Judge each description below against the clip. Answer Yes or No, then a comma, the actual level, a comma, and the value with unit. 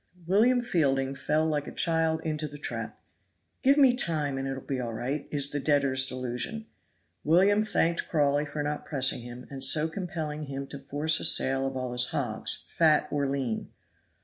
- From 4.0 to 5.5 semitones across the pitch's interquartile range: No, average, 3.1 semitones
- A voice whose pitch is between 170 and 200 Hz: No, medium, 145 Hz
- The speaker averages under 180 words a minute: No, average, 185 wpm